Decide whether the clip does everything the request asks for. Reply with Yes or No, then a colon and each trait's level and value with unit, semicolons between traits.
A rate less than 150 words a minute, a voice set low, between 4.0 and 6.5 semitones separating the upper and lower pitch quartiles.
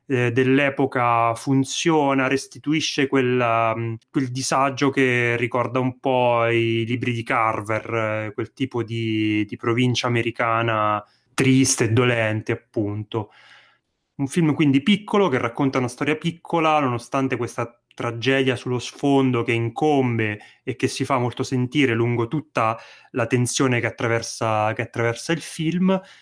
No: average, 130 wpm; low, 125 Hz; average, 2.8 semitones